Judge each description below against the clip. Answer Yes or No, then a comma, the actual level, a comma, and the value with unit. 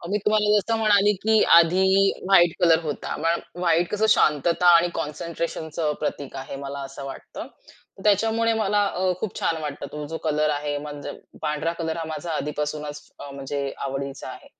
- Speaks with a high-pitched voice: No, medium, 160 Hz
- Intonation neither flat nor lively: Yes, average, 4.3 semitones